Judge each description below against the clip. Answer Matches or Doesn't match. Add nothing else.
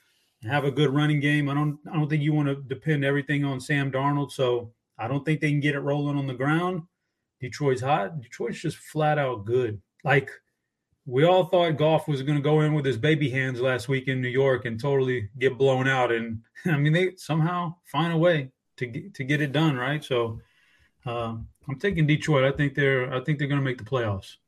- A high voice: Doesn't match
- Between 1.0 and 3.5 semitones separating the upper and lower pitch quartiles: Matches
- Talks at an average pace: Doesn't match